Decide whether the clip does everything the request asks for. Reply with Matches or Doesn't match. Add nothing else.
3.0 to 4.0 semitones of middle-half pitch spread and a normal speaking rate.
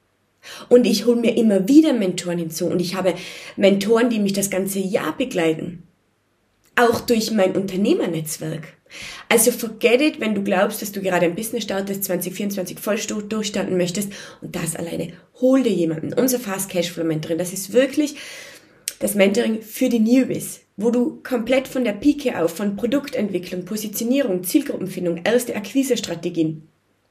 Doesn't match